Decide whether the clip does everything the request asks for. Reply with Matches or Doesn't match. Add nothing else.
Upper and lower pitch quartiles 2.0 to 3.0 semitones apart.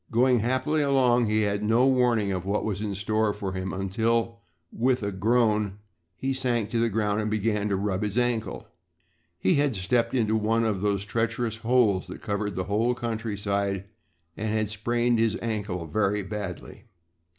Matches